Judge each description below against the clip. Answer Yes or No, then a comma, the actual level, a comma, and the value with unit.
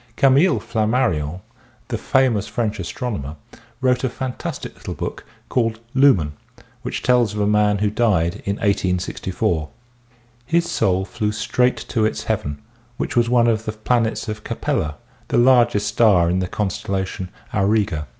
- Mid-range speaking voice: No, low, 105 Hz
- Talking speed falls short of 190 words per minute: Yes, average, 150 wpm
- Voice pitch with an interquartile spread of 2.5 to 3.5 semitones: No, average, 4.2 semitones